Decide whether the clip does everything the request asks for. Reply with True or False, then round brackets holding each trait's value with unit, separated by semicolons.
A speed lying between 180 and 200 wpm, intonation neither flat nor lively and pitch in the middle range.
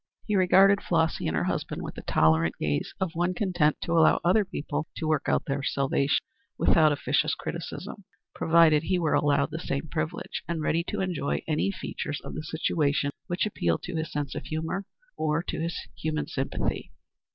True (185 wpm; 3.1 semitones; 160 Hz)